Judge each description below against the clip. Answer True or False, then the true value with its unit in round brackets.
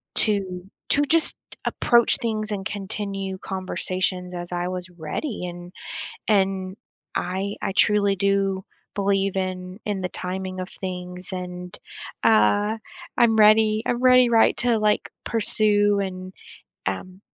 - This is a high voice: True (195 Hz)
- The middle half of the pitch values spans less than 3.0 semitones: True (2.4 semitones)